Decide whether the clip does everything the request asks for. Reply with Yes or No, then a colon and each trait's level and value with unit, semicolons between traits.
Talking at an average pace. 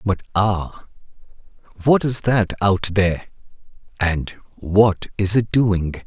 No: slow, 120 wpm